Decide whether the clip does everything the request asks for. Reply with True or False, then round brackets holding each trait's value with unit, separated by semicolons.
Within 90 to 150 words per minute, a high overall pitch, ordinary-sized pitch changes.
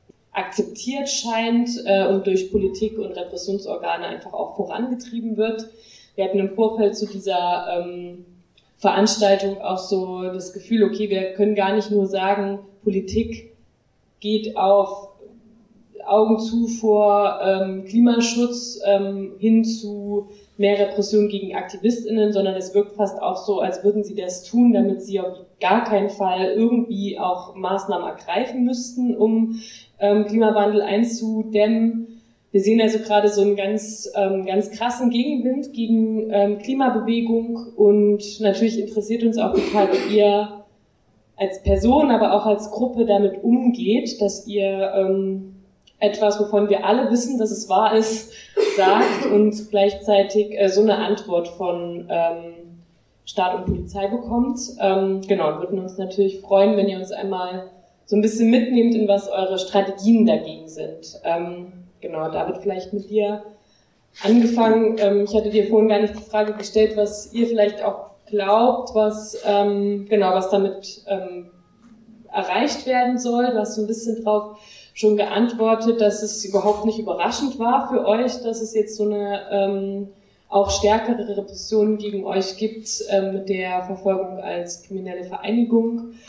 False (145 wpm; 205 Hz; 2.2 semitones)